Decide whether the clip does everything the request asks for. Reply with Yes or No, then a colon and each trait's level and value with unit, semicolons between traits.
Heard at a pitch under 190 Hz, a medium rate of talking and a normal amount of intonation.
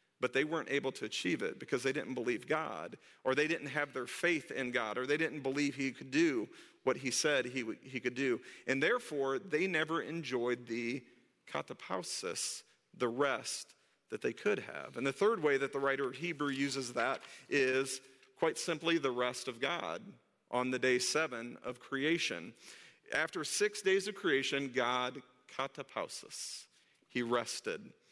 Yes: low, 135 Hz; average, 170 wpm; average, 3.6 semitones